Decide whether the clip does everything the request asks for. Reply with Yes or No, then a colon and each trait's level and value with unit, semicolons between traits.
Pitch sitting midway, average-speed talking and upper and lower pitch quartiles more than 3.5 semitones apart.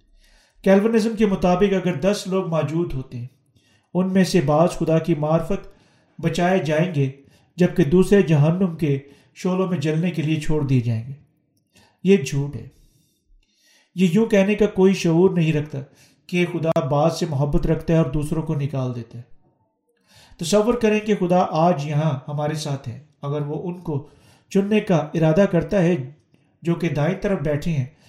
Yes: medium, 160 Hz; average, 175 wpm; average, 4.1 semitones